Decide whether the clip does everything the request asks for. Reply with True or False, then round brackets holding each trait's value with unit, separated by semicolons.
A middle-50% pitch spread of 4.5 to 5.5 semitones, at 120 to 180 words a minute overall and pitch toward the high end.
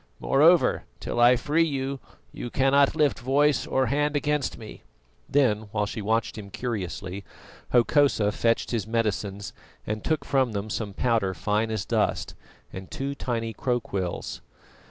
False (4.8 semitones; 145 wpm; 115 Hz)